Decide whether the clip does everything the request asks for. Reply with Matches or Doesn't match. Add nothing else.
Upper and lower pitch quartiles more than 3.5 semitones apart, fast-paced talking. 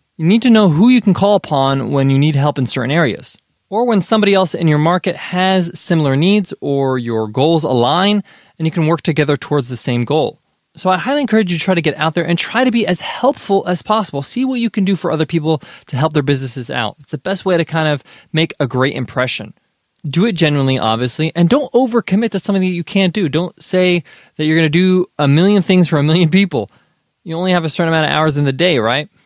Matches